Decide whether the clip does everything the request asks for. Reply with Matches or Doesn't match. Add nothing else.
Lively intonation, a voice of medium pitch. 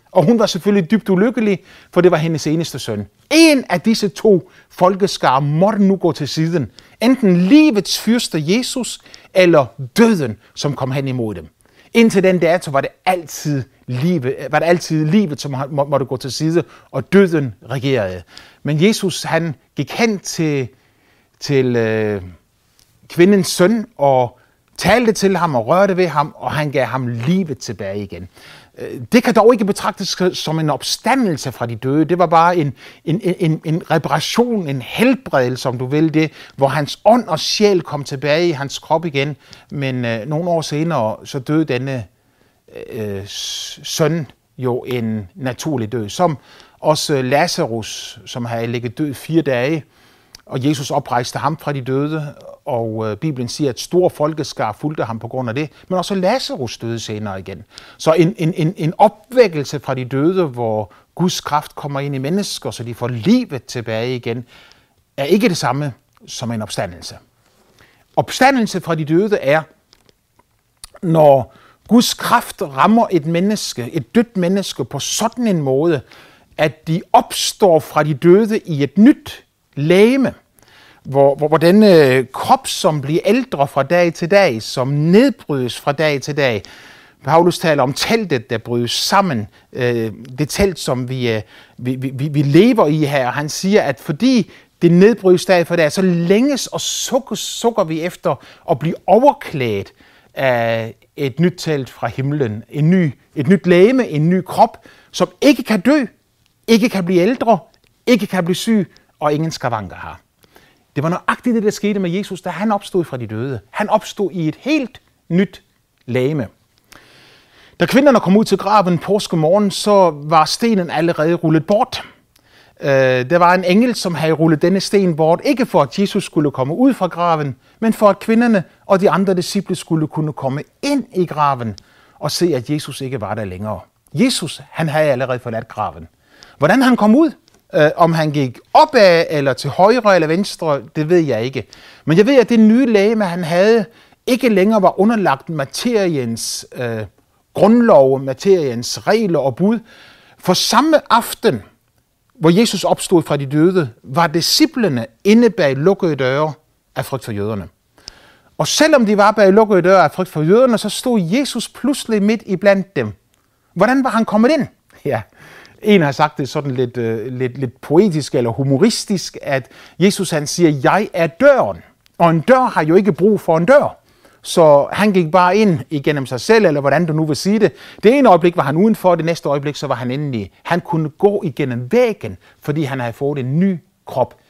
Matches